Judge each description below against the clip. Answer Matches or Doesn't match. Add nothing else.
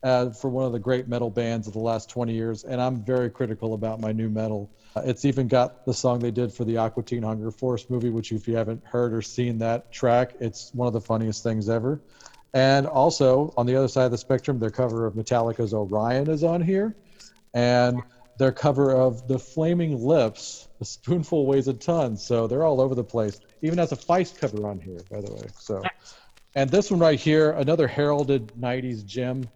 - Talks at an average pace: Doesn't match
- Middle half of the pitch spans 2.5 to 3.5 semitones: Matches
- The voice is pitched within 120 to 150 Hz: Matches